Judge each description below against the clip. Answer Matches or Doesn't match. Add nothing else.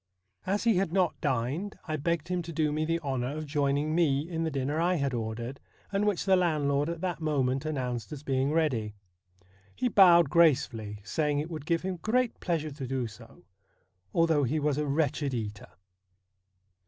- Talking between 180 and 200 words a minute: Matches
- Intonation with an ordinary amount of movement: Matches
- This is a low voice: Doesn't match